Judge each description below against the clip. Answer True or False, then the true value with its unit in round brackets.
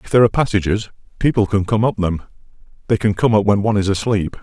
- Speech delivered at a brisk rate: True (230 wpm)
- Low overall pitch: True (105 Hz)